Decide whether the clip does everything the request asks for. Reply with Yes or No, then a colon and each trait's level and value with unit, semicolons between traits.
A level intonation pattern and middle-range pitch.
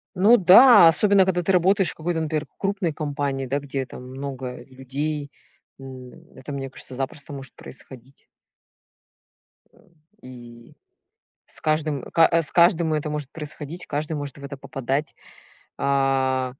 No: average, 3.5 semitones; medium, 145 Hz